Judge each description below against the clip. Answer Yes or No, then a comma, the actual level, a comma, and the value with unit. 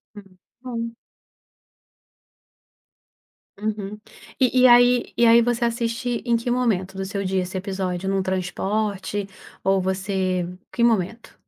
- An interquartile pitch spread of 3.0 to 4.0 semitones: Yes, average, 3.7 semitones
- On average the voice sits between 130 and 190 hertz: No, high, 205 Hz